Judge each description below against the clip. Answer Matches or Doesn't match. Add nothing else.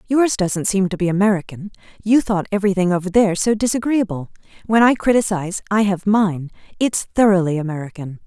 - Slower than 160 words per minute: Matches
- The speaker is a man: Doesn't match